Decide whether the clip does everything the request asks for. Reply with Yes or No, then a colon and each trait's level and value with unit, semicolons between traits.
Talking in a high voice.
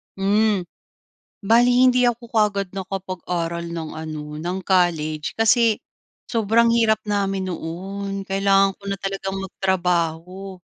Yes: high, 195 Hz